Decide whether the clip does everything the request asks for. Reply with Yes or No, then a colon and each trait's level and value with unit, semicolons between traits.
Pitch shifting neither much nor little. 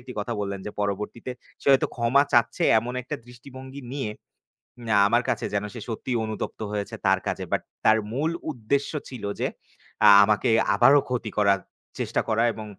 Yes: average, 3.7 semitones